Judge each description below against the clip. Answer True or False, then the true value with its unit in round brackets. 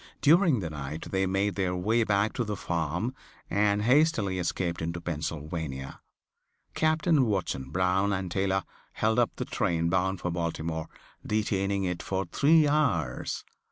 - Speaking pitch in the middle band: False (95 Hz)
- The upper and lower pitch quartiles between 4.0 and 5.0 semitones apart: True (4.3 semitones)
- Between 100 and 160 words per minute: True (145 wpm)